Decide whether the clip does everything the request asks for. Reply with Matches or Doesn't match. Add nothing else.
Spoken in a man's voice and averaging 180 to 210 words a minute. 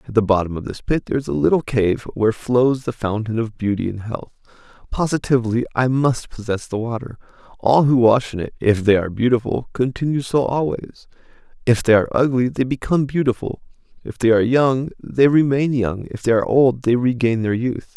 Matches